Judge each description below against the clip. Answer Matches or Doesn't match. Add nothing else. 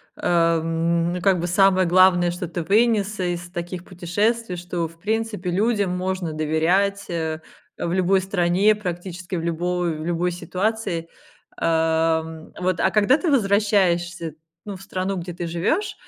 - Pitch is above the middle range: Doesn't match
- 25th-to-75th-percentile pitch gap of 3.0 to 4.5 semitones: Doesn't match